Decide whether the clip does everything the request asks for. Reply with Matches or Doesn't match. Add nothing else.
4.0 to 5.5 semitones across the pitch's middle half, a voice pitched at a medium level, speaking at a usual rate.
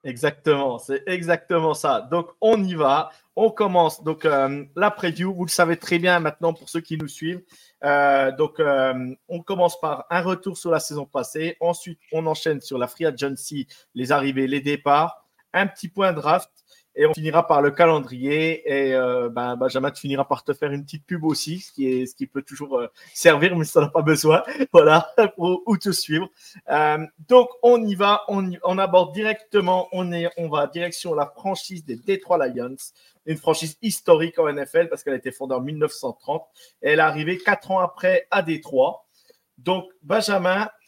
Matches